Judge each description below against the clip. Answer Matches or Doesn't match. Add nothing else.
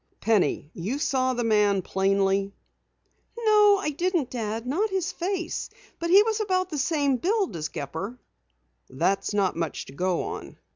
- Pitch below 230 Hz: Doesn't match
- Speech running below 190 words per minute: Matches